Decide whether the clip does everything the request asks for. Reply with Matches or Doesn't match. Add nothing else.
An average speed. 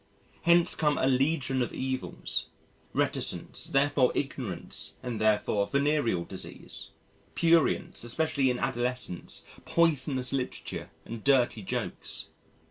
Doesn't match